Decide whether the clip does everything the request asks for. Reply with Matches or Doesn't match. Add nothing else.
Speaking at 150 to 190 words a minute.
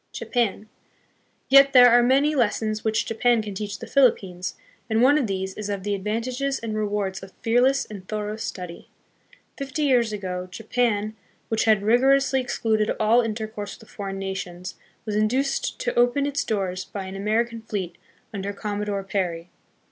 Matches